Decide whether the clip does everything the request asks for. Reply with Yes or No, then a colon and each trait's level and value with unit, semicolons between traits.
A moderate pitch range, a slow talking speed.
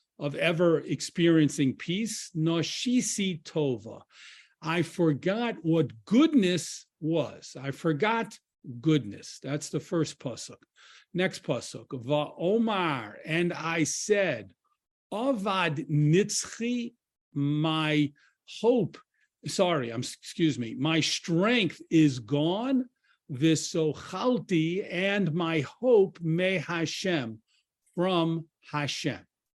Yes: average, 4.4 semitones; slow, 90 wpm